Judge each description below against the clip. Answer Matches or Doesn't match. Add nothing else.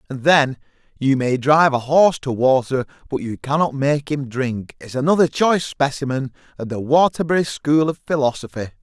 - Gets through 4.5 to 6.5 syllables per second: Matches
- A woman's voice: Doesn't match